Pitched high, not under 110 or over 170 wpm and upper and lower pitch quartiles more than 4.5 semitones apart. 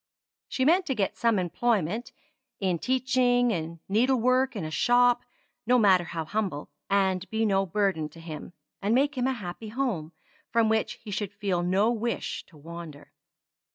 Yes: high, 210 Hz; average, 165 wpm; wide, 5.6 semitones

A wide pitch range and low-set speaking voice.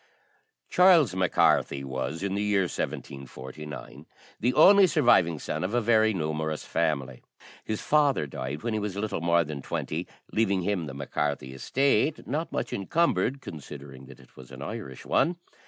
Yes: wide, 8.1 semitones; very low, 90 Hz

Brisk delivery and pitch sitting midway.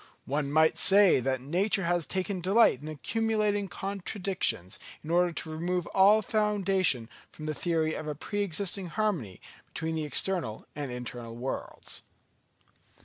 No: average, 145 wpm; medium, 175 Hz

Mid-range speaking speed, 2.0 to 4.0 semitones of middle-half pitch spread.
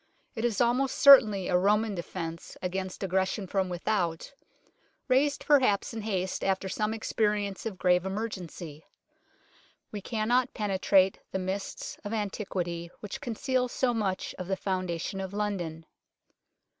No: slow, 130 wpm; average, 3.0 semitones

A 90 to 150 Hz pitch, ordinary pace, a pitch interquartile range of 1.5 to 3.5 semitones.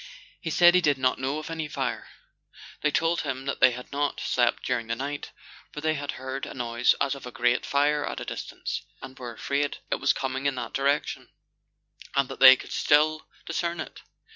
No: medium, 140 Hz; fast, 210 wpm; narrow, 2.4 semitones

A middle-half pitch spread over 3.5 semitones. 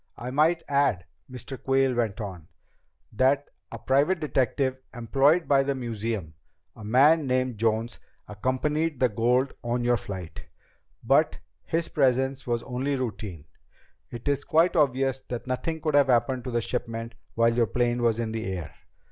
No: average, 3.1 semitones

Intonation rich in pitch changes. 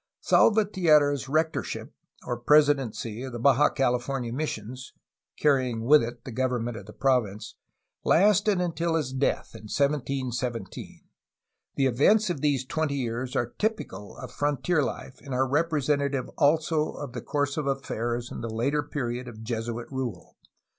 No: average, 3.7 semitones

